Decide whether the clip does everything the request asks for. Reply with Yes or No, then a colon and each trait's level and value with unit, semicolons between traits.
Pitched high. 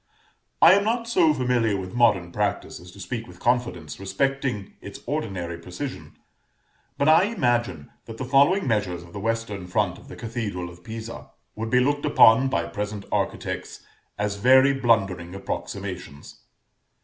No: low, 115 Hz